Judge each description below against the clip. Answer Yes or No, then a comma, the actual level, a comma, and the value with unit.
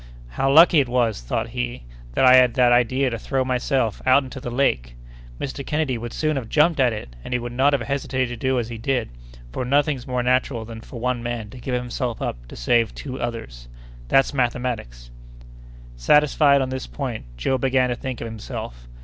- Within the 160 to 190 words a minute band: No, fast, 205 wpm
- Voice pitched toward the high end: No, low, 125 Hz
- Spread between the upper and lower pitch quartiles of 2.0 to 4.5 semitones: Yes, average, 2.7 semitones